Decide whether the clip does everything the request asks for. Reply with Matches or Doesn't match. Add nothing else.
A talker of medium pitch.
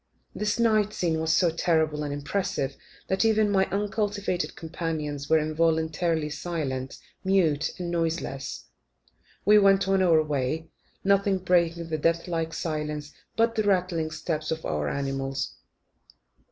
Matches